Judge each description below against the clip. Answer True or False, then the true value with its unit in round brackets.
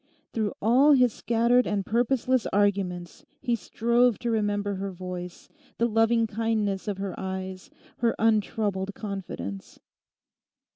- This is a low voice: False (210 Hz)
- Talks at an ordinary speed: False (125 wpm)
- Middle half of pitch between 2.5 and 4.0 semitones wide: True (3.4 semitones)